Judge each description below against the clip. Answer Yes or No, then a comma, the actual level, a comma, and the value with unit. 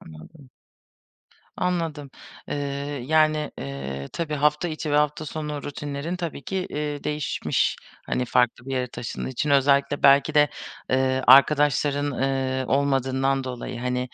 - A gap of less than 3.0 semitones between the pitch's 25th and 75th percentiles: Yes, narrow, 2.4 semitones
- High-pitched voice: No, medium, 140 Hz